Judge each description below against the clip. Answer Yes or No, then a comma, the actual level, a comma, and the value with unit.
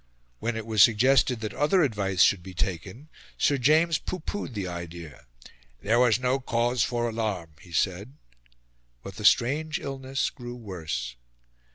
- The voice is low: Yes, low, 115 Hz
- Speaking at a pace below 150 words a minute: No, average, 155 wpm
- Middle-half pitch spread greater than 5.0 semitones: Yes, wide, 5.6 semitones